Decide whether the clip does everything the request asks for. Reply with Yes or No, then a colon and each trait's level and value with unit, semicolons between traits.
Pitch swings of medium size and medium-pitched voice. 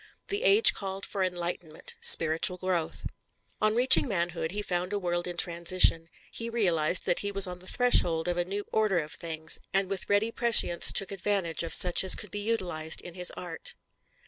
Yes: average, 3.0 semitones; medium, 180 Hz